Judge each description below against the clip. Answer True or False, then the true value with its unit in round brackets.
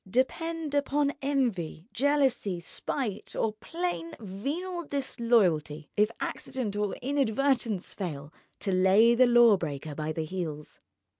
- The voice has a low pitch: False (225 Hz)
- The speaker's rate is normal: False (120 wpm)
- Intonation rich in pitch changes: True (7.3 semitones)